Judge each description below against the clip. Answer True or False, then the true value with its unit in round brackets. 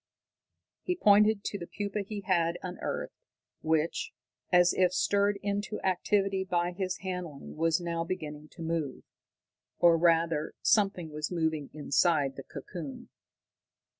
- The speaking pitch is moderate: True (175 Hz)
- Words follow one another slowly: True (130 wpm)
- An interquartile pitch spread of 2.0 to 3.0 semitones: False (3.4 semitones)